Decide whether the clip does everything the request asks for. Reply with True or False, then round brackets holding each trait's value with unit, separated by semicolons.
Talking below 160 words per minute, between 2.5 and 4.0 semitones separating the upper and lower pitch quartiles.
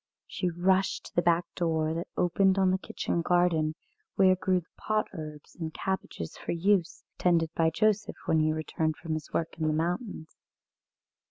False (175 wpm; 2.9 semitones)